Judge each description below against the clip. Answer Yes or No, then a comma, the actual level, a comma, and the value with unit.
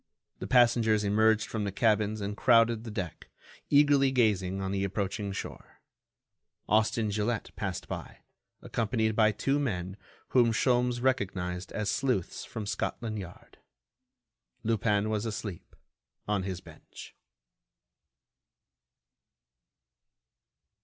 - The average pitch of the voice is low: Yes, low, 110 Hz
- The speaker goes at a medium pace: No, slow, 110 wpm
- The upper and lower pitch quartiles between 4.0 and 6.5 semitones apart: No, average, 2.7 semitones